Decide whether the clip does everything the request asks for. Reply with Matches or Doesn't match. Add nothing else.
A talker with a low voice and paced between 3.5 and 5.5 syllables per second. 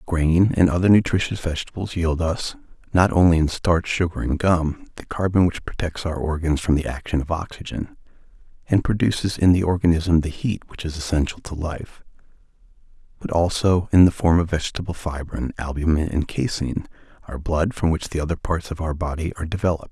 Doesn't match